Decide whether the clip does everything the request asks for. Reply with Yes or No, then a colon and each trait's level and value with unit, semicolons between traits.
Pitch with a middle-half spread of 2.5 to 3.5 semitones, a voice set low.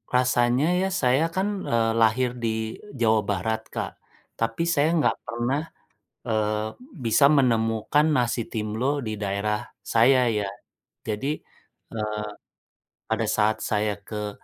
Yes: average, 3.0 semitones; low, 115 Hz